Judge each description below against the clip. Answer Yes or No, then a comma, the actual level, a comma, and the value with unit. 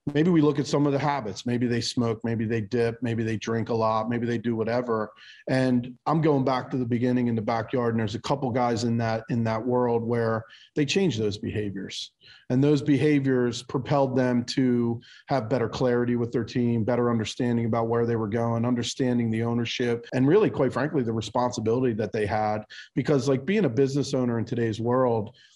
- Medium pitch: No, low, 120 Hz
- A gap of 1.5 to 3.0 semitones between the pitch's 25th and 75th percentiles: Yes, narrow, 2.4 semitones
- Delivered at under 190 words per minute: No, fast, 205 wpm